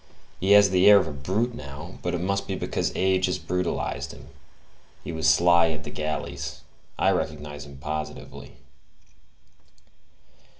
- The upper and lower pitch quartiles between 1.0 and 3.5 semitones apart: No, average, 4.2 semitones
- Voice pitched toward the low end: Yes, very low, 85 Hz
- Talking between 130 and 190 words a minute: Yes, average, 155 wpm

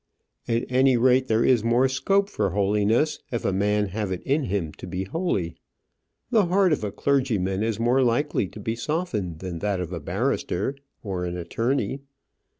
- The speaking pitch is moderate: No, low, 110 Hz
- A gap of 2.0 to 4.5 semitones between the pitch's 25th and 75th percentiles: No, wide, 5.6 semitones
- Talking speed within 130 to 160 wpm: No, average, 180 wpm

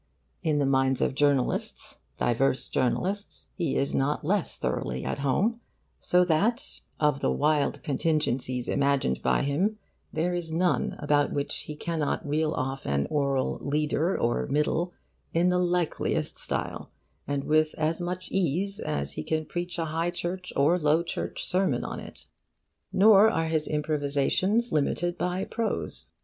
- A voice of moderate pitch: Yes, medium, 155 Hz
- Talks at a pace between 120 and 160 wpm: Yes, average, 150 wpm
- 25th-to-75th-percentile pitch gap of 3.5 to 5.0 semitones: Yes, average, 4.1 semitones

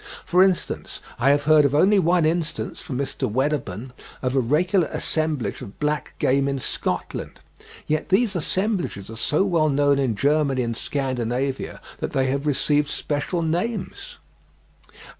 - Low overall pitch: No, medium, 145 Hz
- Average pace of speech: Yes, average, 150 wpm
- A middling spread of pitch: Yes, average, 4.0 semitones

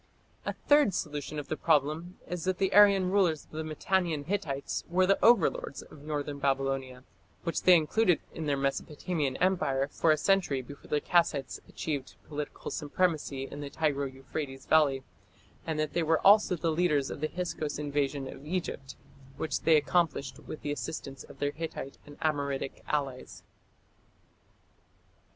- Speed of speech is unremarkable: Yes, average, 160 wpm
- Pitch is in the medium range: Yes, medium, 150 Hz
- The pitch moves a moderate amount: Yes, average, 3.7 semitones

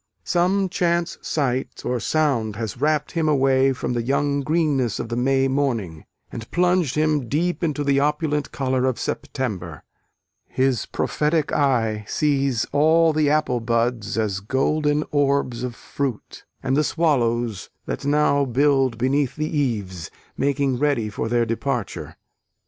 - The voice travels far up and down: No, average, 4.0 semitones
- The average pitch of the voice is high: No, low, 135 Hz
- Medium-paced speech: Yes, average, 145 wpm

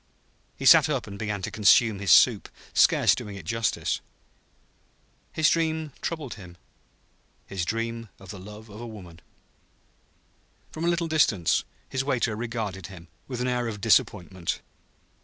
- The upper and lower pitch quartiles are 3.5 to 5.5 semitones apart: Yes, average, 4.2 semitones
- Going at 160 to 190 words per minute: No, average, 145 wpm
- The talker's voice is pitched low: Yes, low, 110 Hz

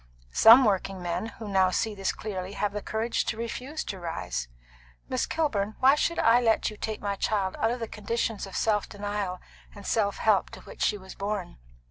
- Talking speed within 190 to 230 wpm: Yes, average, 200 wpm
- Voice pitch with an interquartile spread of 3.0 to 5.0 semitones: No, narrow, 2.6 semitones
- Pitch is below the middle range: No, high, 210 Hz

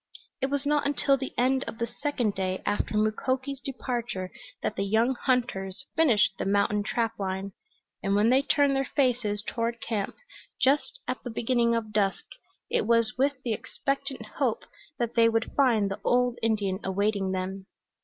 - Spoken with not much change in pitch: No, average, 4.2 semitones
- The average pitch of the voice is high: Yes, high, 230 Hz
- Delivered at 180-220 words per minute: No, average, 170 wpm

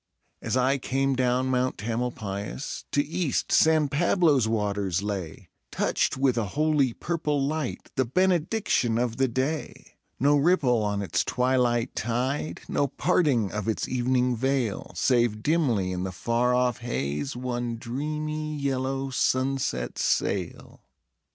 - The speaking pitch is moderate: No, low, 130 Hz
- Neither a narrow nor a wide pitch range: Yes, average, 3.7 semitones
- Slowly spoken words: Yes, slow, 130 wpm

